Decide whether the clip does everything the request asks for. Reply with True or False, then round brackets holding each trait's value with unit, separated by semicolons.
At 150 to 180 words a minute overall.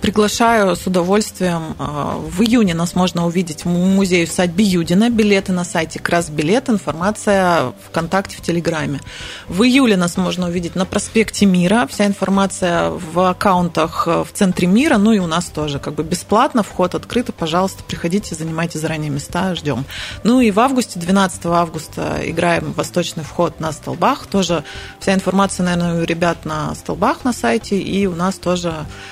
True (160 wpm)